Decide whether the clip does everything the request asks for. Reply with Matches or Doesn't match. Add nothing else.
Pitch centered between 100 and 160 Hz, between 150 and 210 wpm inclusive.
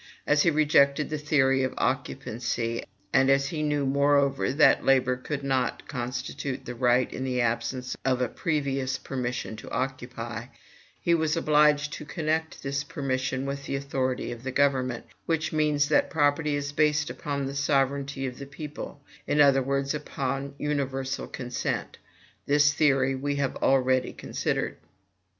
Matches